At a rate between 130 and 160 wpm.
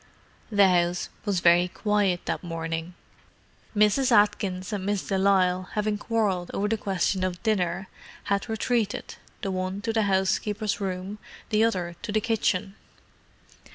Yes: average, 145 wpm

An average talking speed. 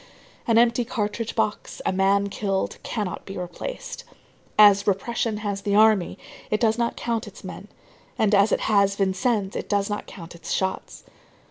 Yes: average, 165 wpm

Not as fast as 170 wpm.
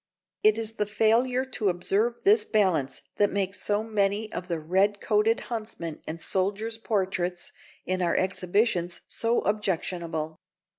Yes: average, 140 wpm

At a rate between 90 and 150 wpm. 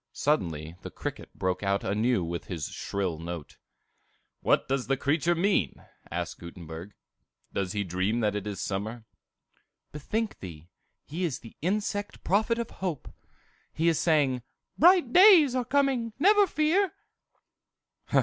Yes: average, 140 wpm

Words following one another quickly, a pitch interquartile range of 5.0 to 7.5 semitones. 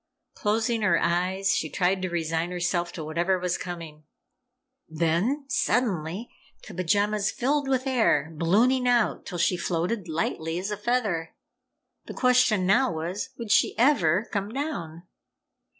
No: average, 140 wpm; wide, 5.5 semitones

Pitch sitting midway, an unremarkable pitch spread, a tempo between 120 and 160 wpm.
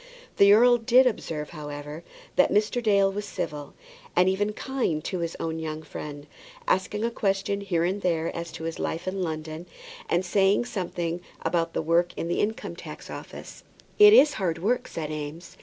No: medium, 180 Hz; average, 4.1 semitones; average, 180 wpm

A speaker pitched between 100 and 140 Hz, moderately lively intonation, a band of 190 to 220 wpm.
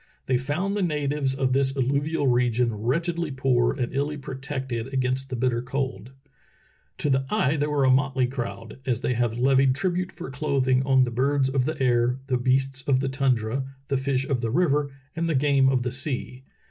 No: low, 135 Hz; narrow, 2.0 semitones; average, 195 wpm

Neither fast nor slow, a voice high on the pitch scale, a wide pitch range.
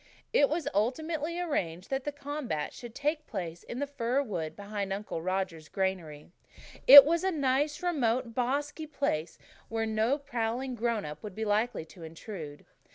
Yes: average, 160 wpm; high, 230 Hz; wide, 7.0 semitones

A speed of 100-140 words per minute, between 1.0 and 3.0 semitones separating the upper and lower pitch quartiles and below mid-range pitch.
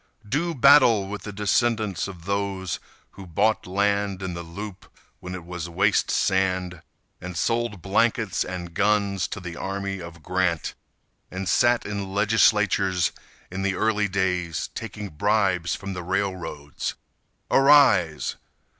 Yes: slow, 135 wpm; narrow, 2.5 semitones; very low, 95 Hz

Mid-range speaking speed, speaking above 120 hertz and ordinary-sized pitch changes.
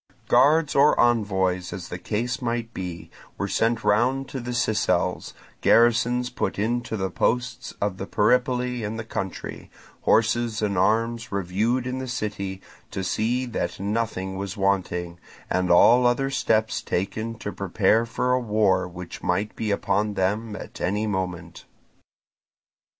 No: average, 145 wpm; low, 110 Hz; average, 3.9 semitones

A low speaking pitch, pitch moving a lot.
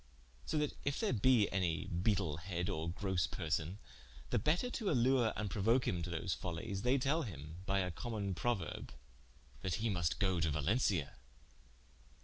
Yes: very low, 95 Hz; wide, 5.9 semitones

